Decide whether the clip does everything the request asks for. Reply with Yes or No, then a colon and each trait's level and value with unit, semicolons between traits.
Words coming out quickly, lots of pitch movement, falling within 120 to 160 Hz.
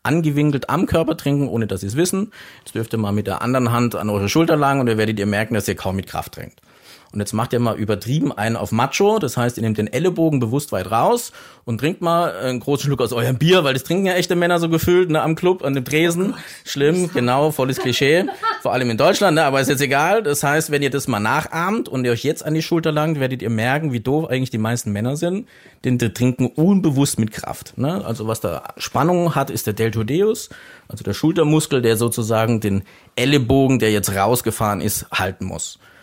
Yes: fast, 230 wpm; wide, 5.7 semitones; low, 135 Hz